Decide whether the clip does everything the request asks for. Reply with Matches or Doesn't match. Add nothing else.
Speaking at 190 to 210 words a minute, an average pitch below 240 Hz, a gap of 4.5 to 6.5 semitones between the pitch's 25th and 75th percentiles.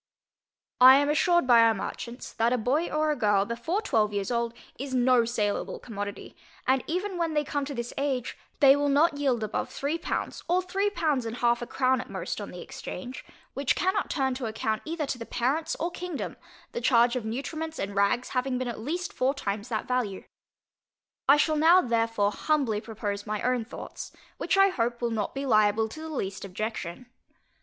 Doesn't match